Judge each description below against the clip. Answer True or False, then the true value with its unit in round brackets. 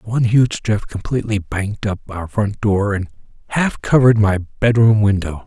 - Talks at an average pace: True (165 wpm)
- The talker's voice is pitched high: False (105 Hz)